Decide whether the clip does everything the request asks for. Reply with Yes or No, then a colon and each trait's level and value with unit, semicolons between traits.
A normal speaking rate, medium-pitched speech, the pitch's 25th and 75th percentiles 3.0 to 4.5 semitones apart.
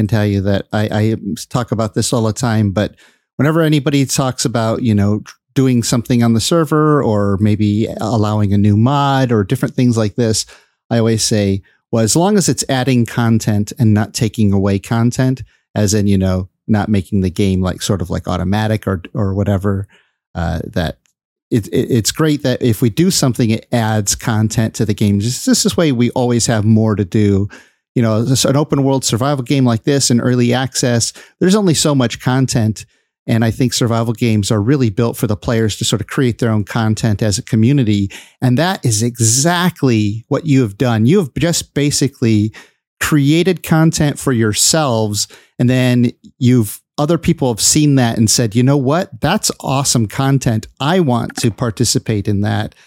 No: average, 190 wpm; low, 120 Hz; average, 3.9 semitones